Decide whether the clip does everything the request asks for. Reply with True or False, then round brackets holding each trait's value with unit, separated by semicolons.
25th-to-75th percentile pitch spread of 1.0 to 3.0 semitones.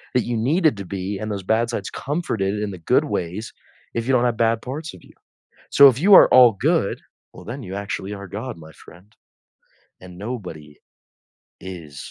False (4.6 semitones)